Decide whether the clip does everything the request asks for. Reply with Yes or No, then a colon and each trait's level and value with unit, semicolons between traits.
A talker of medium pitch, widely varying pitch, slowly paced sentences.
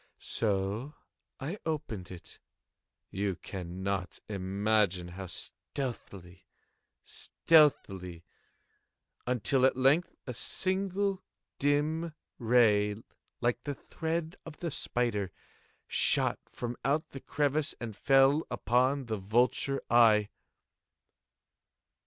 No: low, 120 Hz; wide, 6.7 semitones; slow, 90 wpm